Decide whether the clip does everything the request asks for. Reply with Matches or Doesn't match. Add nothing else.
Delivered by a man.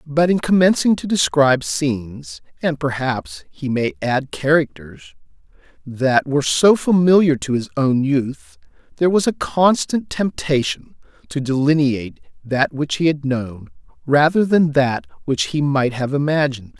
Matches